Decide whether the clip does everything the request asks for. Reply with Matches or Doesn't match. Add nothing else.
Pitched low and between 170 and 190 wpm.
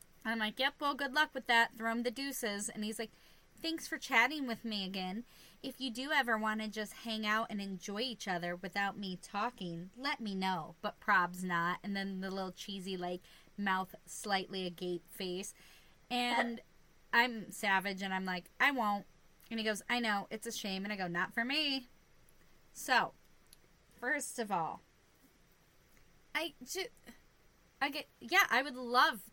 Doesn't match